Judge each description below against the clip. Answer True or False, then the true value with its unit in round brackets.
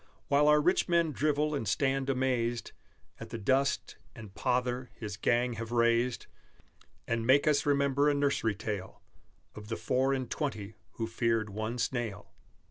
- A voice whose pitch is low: True (125 Hz)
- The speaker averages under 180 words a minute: True (155 wpm)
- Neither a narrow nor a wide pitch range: True (3.7 semitones)